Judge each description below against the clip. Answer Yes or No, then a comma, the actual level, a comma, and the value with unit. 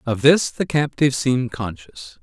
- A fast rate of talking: No, average, 160 wpm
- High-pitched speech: No, low, 125 Hz